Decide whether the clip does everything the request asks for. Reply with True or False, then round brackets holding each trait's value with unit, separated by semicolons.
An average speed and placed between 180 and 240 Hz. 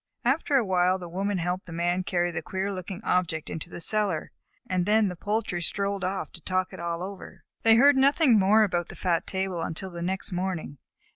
False (210 wpm; 185 Hz)